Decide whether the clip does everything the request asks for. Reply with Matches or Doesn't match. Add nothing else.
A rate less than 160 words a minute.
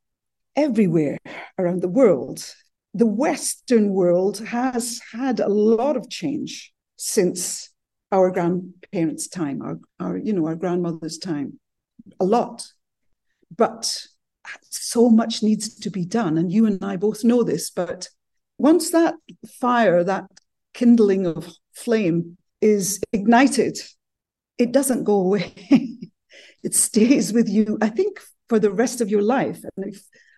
Matches